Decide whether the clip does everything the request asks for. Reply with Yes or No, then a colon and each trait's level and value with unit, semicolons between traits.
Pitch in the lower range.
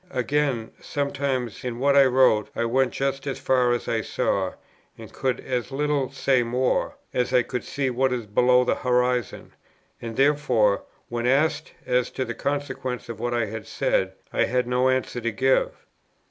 Yes: low, 125 Hz